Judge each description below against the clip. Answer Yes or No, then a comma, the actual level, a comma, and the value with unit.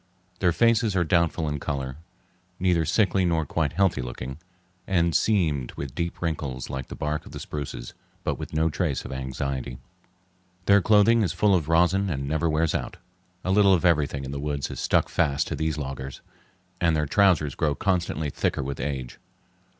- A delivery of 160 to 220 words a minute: Yes, average, 180 wpm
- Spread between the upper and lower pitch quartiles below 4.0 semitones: No, average, 4.3 semitones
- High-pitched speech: No, very low, 80 Hz